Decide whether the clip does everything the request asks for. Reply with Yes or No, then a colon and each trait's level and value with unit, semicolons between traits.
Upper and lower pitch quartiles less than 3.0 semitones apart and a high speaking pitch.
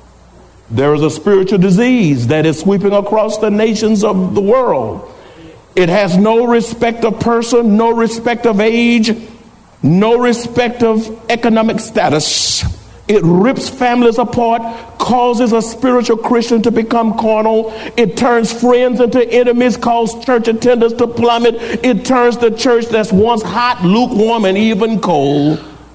Yes: narrow, 2.6 semitones; high, 225 Hz